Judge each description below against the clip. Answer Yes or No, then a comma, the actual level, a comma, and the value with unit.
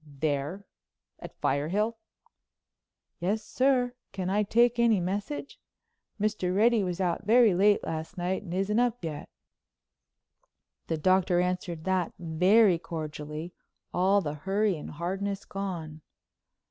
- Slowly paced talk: Yes, slow, 120 wpm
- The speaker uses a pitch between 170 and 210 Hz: Yes, high, 190 Hz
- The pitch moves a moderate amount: Yes, average, 3.9 semitones